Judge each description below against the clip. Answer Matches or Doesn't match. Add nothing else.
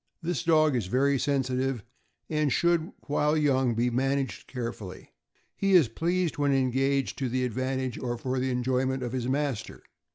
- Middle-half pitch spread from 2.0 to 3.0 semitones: Matches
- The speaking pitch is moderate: Doesn't match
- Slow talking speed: Doesn't match